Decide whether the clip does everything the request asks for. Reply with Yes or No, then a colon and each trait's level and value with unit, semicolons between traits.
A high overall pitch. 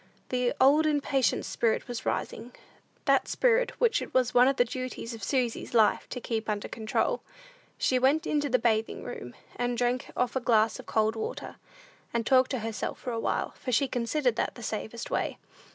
Yes: high, 245 Hz